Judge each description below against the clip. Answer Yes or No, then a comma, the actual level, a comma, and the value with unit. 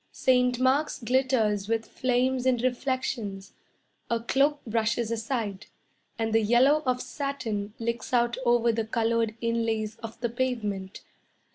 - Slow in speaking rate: Yes, slow, 130 wpm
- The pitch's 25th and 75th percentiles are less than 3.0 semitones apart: Yes, narrow, 2.4 semitones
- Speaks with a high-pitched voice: Yes, high, 235 Hz